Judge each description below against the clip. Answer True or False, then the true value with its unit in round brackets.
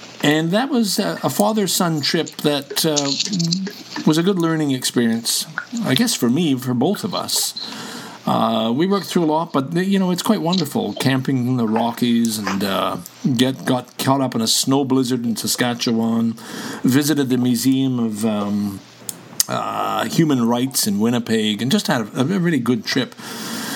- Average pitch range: False (6.3 semitones)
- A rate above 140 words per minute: True (170 wpm)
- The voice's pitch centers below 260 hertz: True (135 Hz)